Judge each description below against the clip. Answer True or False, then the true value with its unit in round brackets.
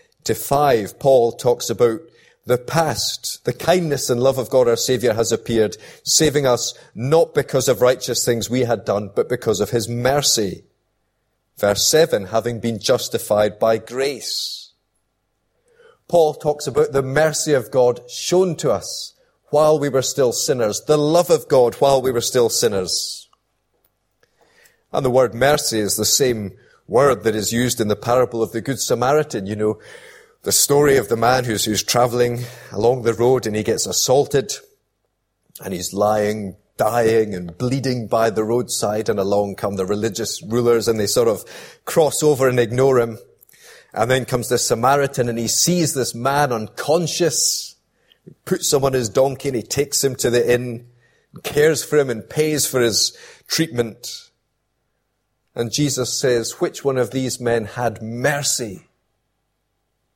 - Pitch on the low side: True (125 Hz)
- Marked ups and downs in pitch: False (4.3 semitones)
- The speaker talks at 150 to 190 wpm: True (165 wpm)